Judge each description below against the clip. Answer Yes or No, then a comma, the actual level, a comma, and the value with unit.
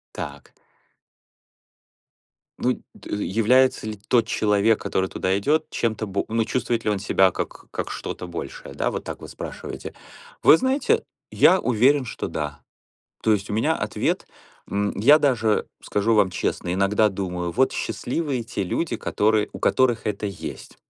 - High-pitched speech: No, low, 110 Hz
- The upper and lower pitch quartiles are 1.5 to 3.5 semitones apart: No, average, 4.0 semitones